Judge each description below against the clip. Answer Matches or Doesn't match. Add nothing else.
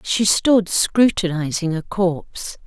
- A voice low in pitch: Doesn't match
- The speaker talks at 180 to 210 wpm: Doesn't match